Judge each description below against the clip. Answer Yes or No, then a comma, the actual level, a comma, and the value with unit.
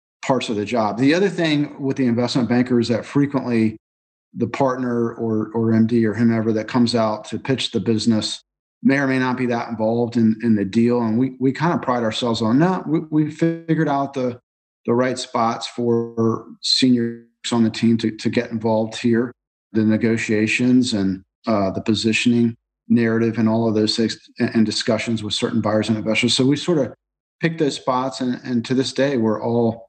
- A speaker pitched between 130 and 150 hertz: No, low, 115 Hz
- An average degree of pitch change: No, narrow, 2.3 semitones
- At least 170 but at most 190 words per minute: No, average, 200 wpm